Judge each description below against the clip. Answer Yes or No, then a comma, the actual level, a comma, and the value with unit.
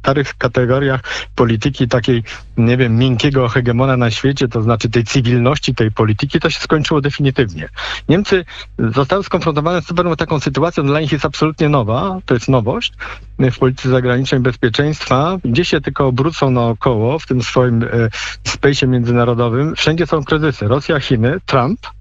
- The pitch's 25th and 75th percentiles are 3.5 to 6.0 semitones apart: Yes, average, 3.9 semitones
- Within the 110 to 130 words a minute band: No, fast, 160 wpm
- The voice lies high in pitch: No, low, 130 Hz